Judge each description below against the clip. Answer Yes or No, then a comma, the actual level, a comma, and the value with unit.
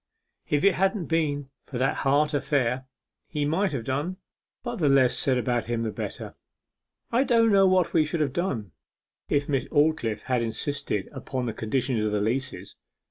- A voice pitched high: No, medium, 140 Hz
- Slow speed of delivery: No, average, 180 wpm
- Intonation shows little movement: No, average, 4.7 semitones